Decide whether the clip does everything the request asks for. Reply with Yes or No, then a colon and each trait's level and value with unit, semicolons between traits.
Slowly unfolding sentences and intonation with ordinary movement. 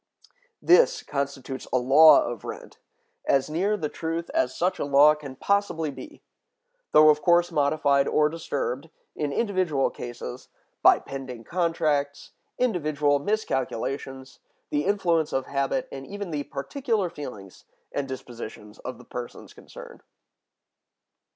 Yes: slow, 130 wpm; average, 4.2 semitones